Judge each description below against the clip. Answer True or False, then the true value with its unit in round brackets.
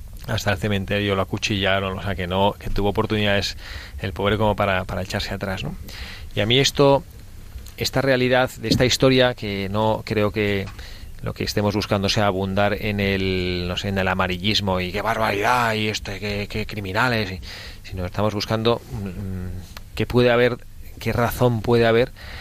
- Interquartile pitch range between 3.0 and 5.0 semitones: False (2.5 semitones)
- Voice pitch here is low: True (100 Hz)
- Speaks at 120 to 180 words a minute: True (175 wpm)